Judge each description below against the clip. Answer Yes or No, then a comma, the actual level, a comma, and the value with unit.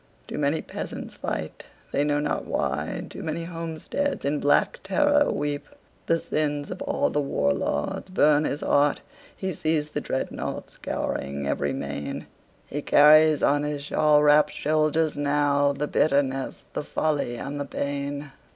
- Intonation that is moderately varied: No, narrow, 1.6 semitones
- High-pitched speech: No, medium, 145 Hz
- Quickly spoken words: No, slow, 135 wpm